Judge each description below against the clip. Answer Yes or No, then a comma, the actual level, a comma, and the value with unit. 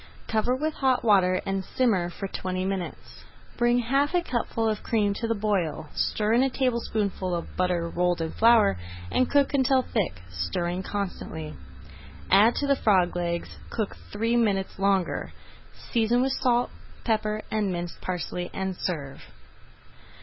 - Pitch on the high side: Yes, high, 205 Hz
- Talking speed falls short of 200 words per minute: Yes, average, 150 wpm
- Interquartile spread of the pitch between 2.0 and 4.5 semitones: No, average, 4.9 semitones